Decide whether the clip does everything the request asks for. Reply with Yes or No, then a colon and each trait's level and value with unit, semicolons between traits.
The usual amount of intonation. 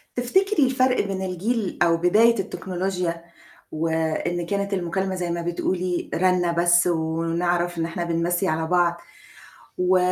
No: narrow, 2.0 semitones